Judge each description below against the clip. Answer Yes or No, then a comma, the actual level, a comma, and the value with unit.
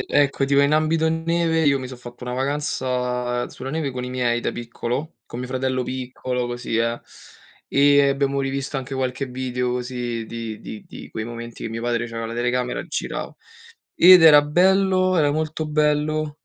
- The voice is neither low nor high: No, low, 130 Hz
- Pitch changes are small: No, average, 3.3 semitones